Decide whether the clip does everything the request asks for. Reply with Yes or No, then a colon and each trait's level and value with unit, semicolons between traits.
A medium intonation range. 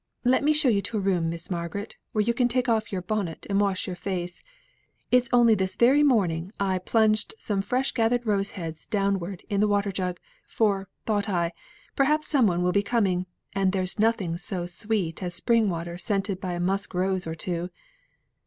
Yes: average, 3.7 semitones